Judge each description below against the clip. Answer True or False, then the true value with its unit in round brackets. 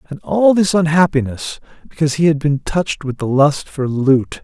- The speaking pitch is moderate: True (150 Hz)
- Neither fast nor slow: True (190 wpm)